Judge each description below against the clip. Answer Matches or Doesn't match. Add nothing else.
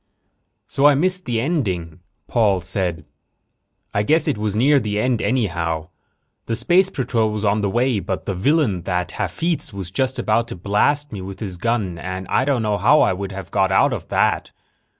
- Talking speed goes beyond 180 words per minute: Matches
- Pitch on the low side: Matches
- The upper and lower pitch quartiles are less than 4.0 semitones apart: Doesn't match